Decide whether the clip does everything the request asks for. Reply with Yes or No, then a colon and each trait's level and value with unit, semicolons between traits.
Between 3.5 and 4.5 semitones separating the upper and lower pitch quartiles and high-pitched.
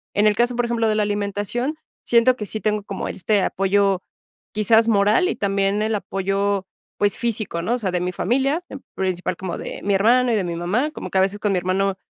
No: average, 3.0 semitones; high, 205 Hz